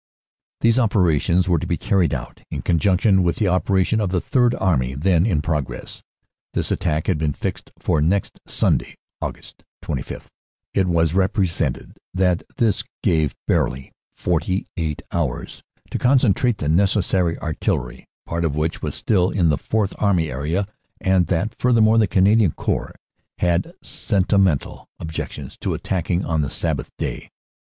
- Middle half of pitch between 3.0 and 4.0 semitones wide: Yes, average, 3.7 semitones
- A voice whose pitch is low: Yes, very low, 90 Hz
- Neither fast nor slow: Yes, average, 150 wpm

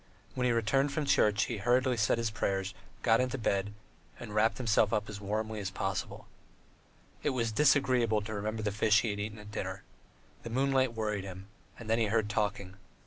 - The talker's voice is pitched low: Yes, low, 110 Hz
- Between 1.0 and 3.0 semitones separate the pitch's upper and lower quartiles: Yes, narrow, 2.4 semitones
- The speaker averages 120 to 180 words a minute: No, average, 195 wpm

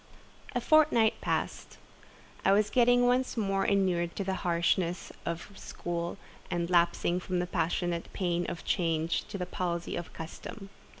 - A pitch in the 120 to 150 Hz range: No, medium, 180 Hz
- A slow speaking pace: No, average, 145 wpm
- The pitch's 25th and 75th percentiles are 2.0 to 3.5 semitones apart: Yes, average, 2.7 semitones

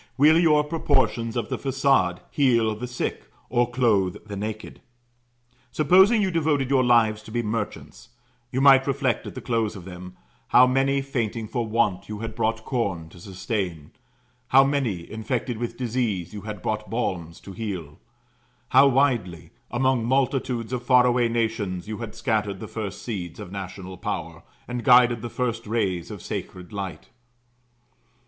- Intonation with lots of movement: No, average, 4.3 semitones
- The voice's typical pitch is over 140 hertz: No, low, 115 Hz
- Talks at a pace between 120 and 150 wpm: No, average, 160 wpm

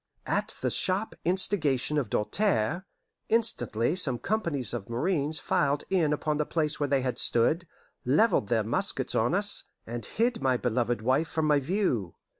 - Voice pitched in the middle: Yes, medium, 145 Hz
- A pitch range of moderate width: No, wide, 6.8 semitones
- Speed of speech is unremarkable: Yes, average, 160 wpm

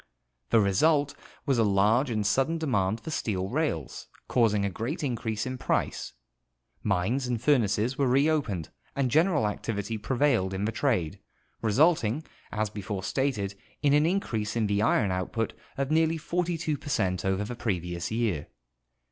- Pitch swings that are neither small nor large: No, wide, 5.9 semitones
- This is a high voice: No, low, 115 Hz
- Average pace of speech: Yes, average, 155 wpm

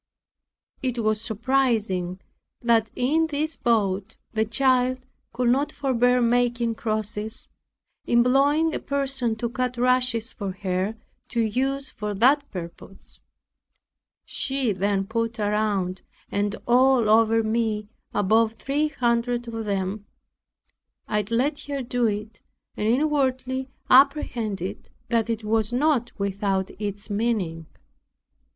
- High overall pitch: Yes, high, 230 Hz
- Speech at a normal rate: No, slow, 115 wpm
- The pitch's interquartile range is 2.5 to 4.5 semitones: Yes, average, 3.4 semitones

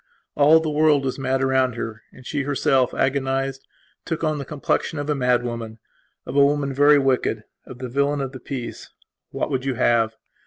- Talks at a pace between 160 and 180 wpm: No, average, 195 wpm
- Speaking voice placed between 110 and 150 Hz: Yes, low, 135 Hz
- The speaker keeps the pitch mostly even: Yes, narrow, 2.1 semitones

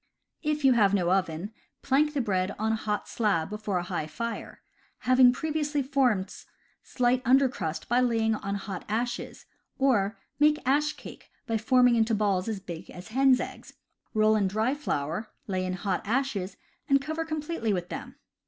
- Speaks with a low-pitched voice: No, high, 225 Hz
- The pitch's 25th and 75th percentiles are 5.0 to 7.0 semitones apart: Yes, average, 5.3 semitones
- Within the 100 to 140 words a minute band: No, average, 170 wpm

